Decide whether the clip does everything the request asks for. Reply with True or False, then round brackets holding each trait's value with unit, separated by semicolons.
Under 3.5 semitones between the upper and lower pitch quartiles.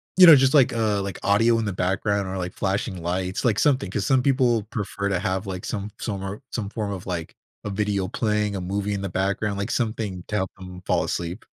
True (2.6 semitones)